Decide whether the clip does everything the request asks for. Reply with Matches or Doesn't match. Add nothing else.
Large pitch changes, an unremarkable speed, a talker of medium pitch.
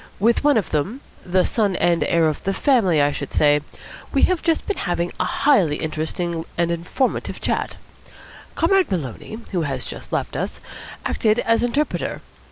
Matches